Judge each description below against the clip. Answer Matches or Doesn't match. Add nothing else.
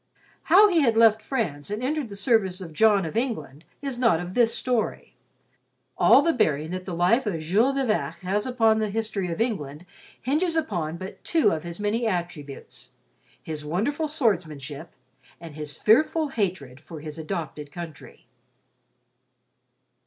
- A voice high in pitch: Matches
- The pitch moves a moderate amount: Doesn't match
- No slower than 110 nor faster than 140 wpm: Doesn't match